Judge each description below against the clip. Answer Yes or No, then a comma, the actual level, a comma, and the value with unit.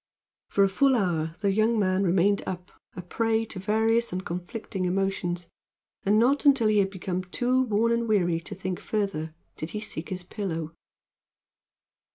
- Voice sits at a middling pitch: No, high, 195 Hz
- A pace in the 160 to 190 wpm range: Yes, average, 170 wpm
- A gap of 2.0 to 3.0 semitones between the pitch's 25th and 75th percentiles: No, average, 3.7 semitones